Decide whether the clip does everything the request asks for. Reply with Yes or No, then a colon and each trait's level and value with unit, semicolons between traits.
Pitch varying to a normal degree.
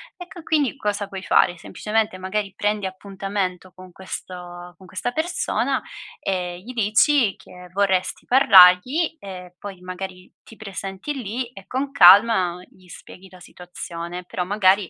Yes: average, 3.0 semitones